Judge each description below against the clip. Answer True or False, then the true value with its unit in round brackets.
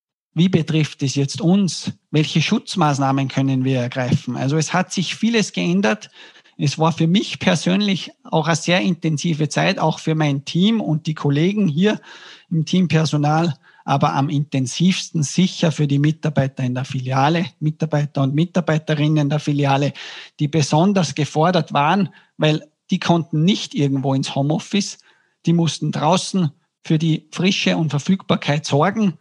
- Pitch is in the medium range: True (160 Hz)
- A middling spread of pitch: True (3.8 semitones)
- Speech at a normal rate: True (145 wpm)